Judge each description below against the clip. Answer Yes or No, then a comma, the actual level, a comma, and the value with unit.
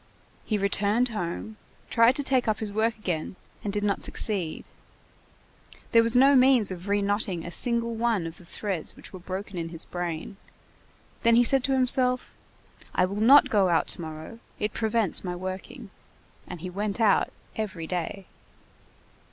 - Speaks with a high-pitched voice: Yes, high, 205 Hz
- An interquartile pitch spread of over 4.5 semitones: No, average, 4.2 semitones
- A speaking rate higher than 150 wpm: Yes, average, 170 wpm